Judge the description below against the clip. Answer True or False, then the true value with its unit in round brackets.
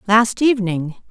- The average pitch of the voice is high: True (210 Hz)